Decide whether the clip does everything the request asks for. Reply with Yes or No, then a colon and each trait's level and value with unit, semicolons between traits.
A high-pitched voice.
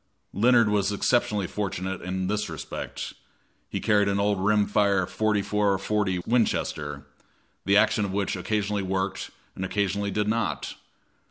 No: low, 100 Hz